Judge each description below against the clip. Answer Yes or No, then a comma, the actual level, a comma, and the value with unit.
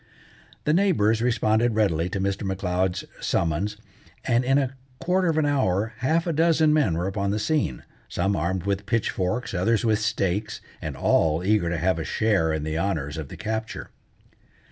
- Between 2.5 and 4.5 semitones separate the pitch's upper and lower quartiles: No, average, 5.3 semitones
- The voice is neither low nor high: No, low, 105 Hz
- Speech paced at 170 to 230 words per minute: Yes, average, 175 wpm